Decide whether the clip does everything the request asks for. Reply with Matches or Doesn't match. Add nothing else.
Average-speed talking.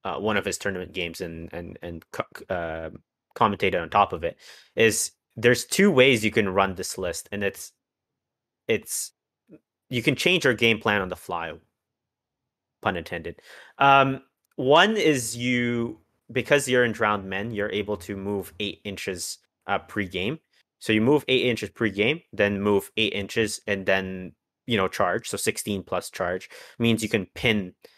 Matches